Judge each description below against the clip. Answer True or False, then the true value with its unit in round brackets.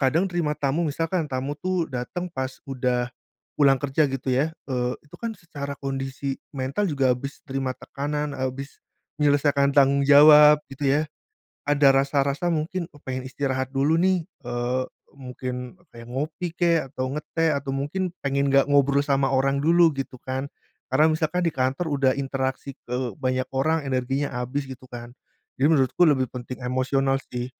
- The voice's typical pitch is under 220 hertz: True (140 Hz)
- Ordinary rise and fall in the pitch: False (2.3 semitones)